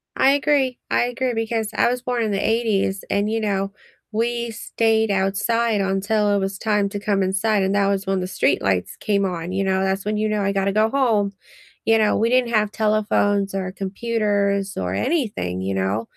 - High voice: Yes, high, 205 Hz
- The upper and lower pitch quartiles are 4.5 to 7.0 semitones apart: No, narrow, 2.5 semitones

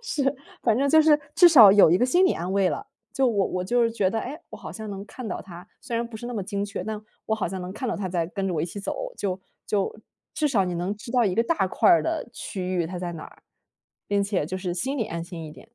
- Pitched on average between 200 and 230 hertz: Yes, high, 205 Hz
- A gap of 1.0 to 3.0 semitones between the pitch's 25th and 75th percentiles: No, average, 5.0 semitones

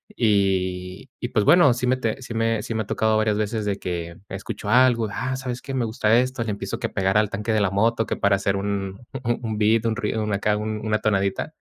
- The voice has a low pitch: Yes, low, 110 Hz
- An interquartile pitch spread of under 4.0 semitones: Yes, narrow, 2.5 semitones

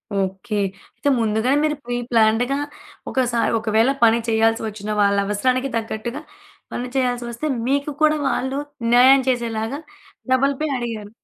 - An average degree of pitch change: Yes, average, 3.1 semitones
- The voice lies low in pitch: No, high, 235 Hz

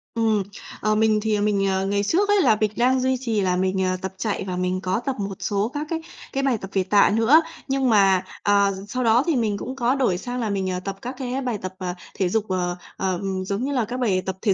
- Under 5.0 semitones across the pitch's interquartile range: Yes, average, 4.6 semitones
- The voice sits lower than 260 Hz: Yes, high, 210 Hz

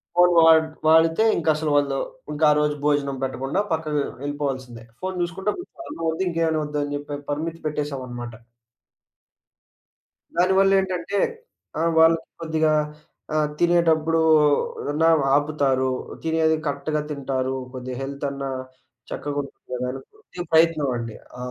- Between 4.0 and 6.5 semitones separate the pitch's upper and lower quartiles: No, average, 2.8 semitones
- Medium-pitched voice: Yes, medium, 150 Hz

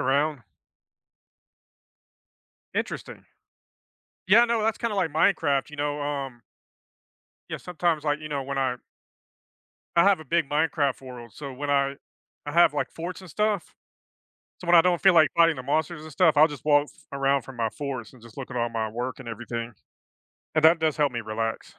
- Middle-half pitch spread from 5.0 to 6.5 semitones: No, average, 4.0 semitones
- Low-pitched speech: No, medium, 145 Hz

